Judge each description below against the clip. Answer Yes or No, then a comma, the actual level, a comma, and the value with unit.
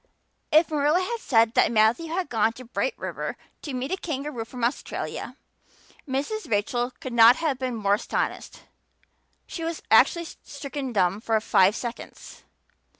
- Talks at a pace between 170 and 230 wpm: No, average, 150 wpm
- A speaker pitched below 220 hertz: No, very high, 255 Hz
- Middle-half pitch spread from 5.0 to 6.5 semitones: Yes, wide, 5.5 semitones